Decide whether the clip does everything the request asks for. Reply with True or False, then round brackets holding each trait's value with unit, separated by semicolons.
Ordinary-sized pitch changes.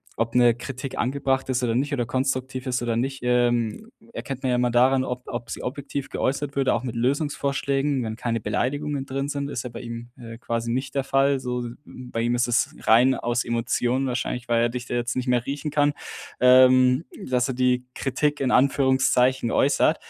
False (2.0 semitones)